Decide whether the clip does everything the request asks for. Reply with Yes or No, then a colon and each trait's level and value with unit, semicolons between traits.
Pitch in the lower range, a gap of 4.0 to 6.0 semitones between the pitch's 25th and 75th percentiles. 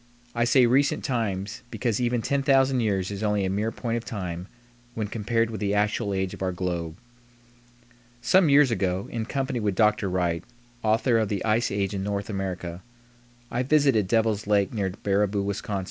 No: low, 105 Hz; average, 3.4 semitones